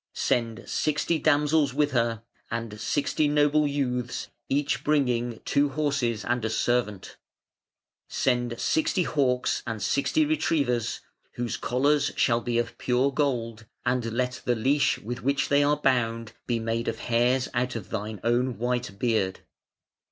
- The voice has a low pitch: Yes, low, 125 Hz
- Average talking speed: Yes, average, 145 wpm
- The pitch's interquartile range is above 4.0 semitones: No, average, 3.4 semitones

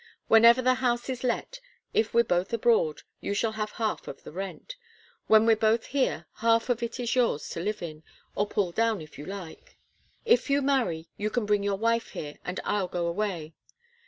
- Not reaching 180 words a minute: No, average, 200 wpm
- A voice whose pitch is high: Yes, high, 220 Hz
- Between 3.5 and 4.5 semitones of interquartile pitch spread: Yes, average, 4.1 semitones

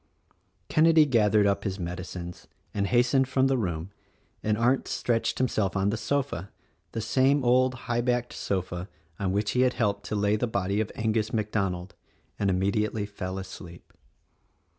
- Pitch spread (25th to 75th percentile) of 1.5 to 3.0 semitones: No, average, 4.1 semitones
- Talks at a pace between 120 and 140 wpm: No, average, 165 wpm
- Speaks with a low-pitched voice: Yes, low, 105 Hz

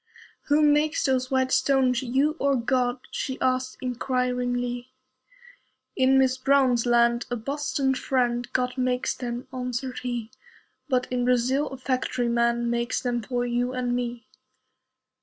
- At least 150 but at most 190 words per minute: No, average, 140 wpm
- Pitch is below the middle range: No, very high, 250 Hz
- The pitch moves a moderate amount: No, narrow, 1.3 semitones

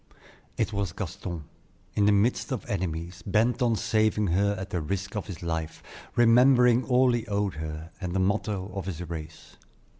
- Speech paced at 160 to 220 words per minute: Yes, average, 175 wpm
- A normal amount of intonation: Yes, average, 4.0 semitones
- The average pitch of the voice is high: No, low, 100 Hz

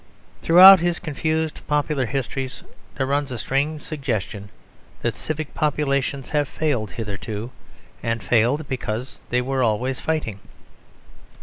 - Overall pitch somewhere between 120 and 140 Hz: Yes, low, 135 Hz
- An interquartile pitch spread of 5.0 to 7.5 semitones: No, average, 4.2 semitones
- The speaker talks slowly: Yes, slow, 120 wpm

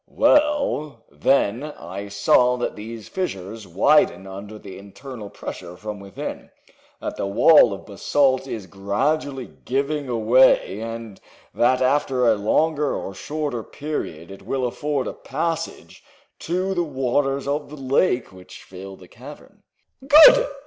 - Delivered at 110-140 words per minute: Yes, slow, 135 wpm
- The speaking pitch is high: No, low, 125 Hz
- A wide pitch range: Yes, wide, 6.5 semitones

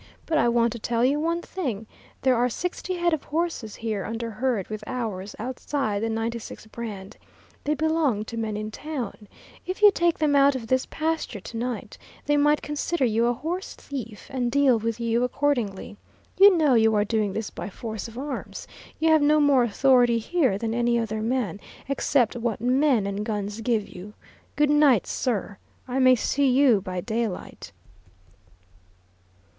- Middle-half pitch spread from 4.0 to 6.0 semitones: Yes, average, 4.7 semitones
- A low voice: No, high, 240 Hz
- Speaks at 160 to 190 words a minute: Yes, average, 175 wpm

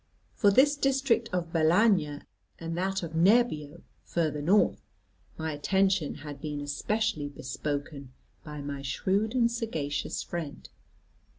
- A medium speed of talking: No, slow, 120 wpm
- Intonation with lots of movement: Yes, wide, 6.3 semitones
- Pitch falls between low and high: Yes, medium, 165 Hz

